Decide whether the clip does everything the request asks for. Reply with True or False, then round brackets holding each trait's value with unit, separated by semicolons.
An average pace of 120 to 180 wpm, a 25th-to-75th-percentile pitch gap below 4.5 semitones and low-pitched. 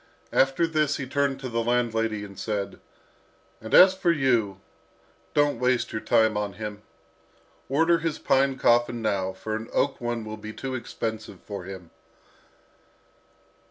True (150 wpm; 4.0 semitones; 120 Hz)